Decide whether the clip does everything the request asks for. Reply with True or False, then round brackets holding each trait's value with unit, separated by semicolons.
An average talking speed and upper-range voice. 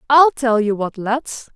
True (195 wpm; 245 Hz)